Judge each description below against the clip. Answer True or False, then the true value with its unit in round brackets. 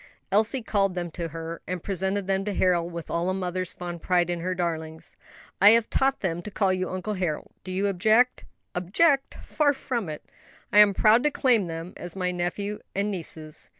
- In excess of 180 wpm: True (200 wpm)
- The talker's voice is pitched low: False (185 Hz)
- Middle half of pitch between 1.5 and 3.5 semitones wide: True (3.2 semitones)